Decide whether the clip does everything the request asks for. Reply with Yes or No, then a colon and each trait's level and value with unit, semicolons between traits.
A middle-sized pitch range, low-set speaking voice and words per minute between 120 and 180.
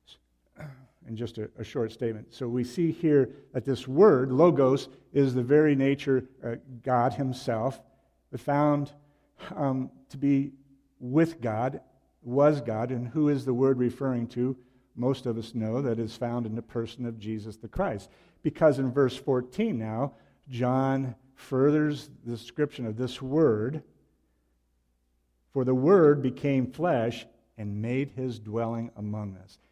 Yes: average, 3.2 semitones; low, 130 Hz; average, 150 wpm